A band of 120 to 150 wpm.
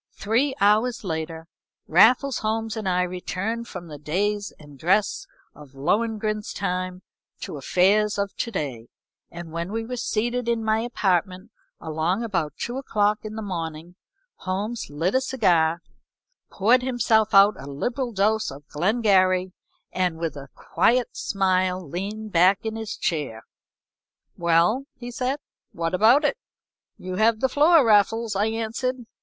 Yes: average, 145 wpm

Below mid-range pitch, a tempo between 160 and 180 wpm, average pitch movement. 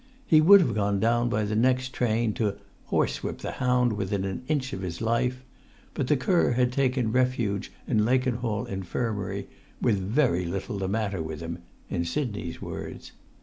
Yes: low, 115 Hz; average, 170 wpm; average, 4.2 semitones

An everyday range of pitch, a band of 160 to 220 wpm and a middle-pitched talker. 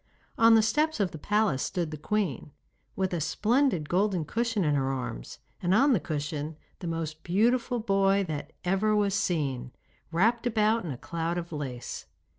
No: wide, 5.8 semitones; average, 175 wpm; medium, 180 Hz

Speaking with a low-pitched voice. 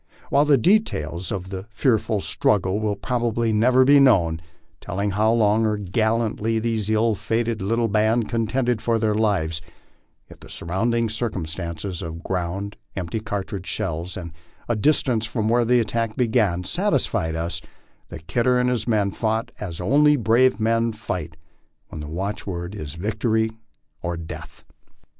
Yes: low, 110 Hz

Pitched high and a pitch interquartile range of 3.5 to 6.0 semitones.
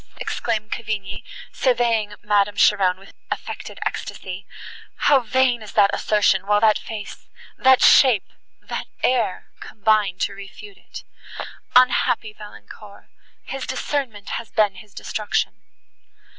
No: high, 215 Hz; average, 3.0 semitones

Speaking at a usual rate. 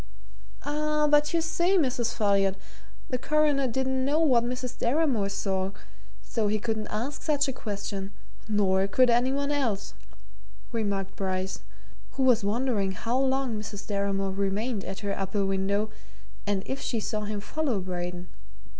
Yes: average, 150 wpm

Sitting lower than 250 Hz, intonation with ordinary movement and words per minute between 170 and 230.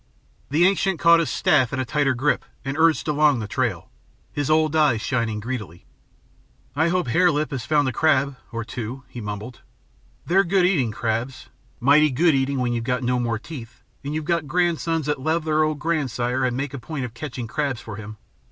Yes: medium, 140 Hz; average, 4.5 semitones; average, 200 wpm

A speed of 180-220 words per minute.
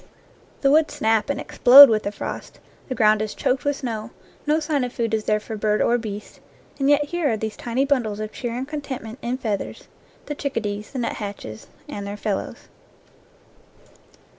Yes: average, 190 wpm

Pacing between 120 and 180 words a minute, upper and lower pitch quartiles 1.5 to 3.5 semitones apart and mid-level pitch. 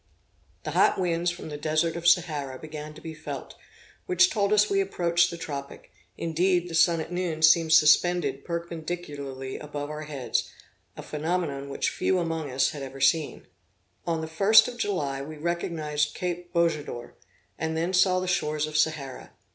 Yes: average, 170 wpm; average, 2.8 semitones; medium, 160 Hz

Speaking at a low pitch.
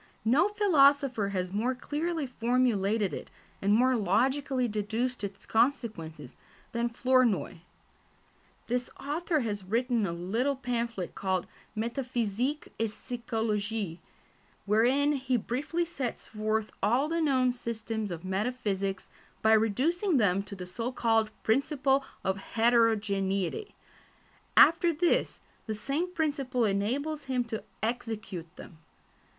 No: high, 235 Hz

